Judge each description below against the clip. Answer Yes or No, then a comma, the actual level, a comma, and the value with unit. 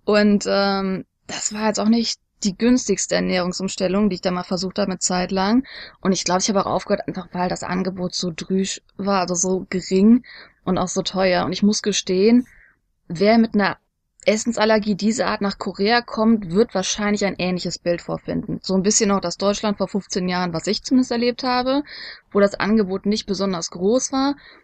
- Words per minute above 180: Yes, fast, 190 wpm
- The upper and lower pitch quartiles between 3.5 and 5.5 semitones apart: No, average, 2.7 semitones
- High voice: Yes, high, 195 Hz